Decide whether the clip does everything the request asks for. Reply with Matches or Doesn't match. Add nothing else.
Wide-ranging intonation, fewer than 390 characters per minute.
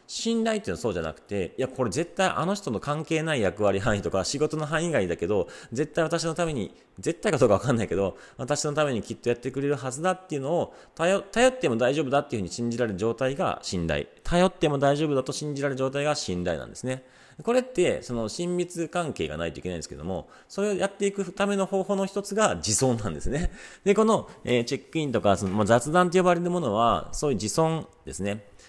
Doesn't match